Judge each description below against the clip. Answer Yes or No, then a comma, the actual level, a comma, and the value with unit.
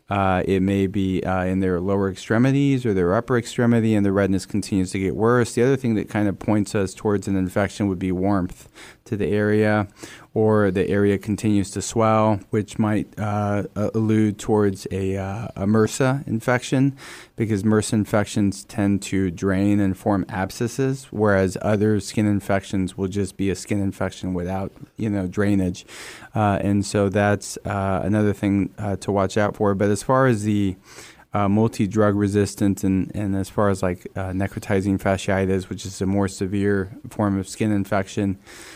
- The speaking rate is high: No, average, 175 wpm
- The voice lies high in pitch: No, low, 100 Hz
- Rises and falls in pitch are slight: Yes, narrow, 1.9 semitones